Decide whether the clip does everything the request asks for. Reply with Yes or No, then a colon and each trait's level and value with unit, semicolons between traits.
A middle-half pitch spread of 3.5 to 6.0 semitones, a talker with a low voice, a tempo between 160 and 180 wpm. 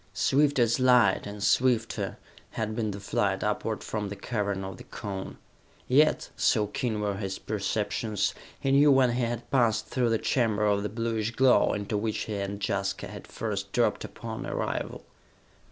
No: average, 3.1 semitones; low, 110 Hz; average, 170 wpm